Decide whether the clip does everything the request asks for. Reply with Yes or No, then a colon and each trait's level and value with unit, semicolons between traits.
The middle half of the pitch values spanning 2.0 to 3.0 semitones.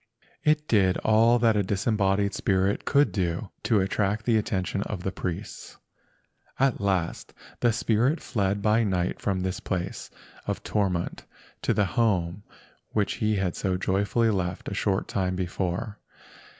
Yes: average, 2.7 semitones